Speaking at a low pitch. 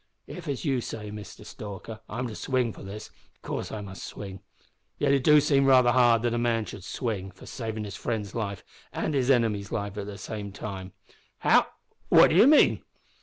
Yes: low, 110 Hz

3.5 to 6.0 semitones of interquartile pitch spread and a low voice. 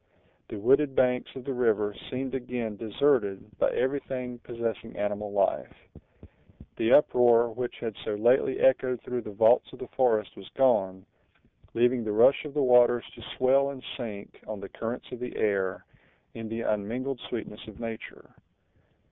No: average, 3.1 semitones; low, 120 Hz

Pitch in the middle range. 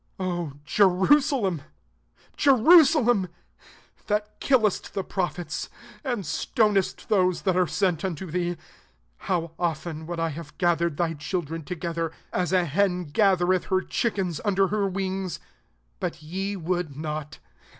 Yes: medium, 180 Hz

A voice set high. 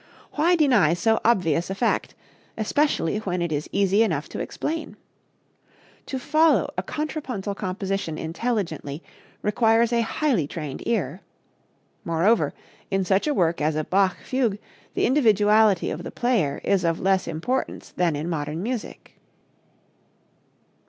Yes: high, 195 Hz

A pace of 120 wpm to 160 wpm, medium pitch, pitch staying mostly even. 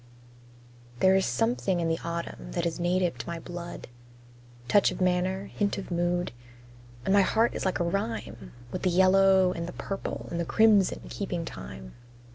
No: average, 175 wpm; medium, 180 Hz; narrow, 2.2 semitones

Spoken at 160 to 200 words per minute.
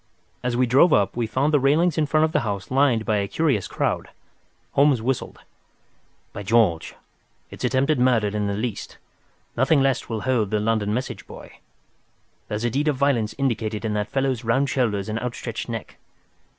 Yes: average, 180 wpm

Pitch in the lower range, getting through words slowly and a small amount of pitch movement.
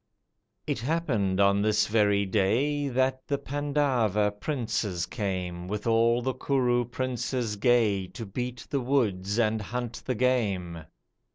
No: low, 115 Hz; slow, 130 wpm; average, 4.2 semitones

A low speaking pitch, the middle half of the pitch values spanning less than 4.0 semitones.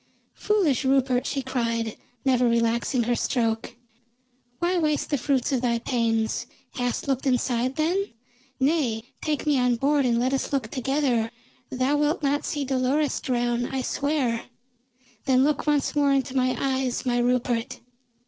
No: very high, 260 Hz; average, 2.9 semitones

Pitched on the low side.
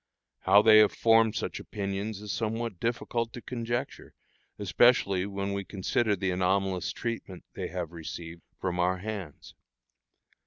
Yes: low, 100 Hz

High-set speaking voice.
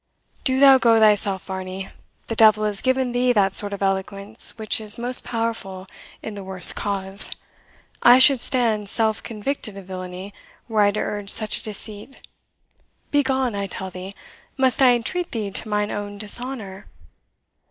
Yes: high, 210 Hz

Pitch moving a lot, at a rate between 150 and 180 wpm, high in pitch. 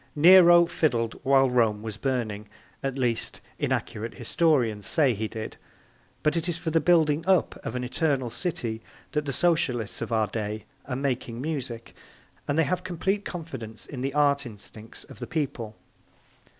No: wide, 5.9 semitones; average, 165 wpm; low, 135 Hz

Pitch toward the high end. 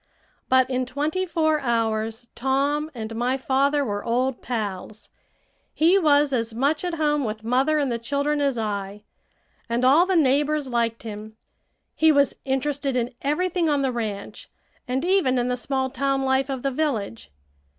Yes: very high, 265 Hz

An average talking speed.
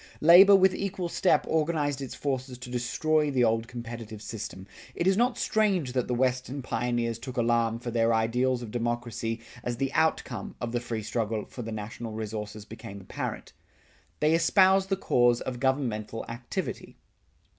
Yes: average, 165 wpm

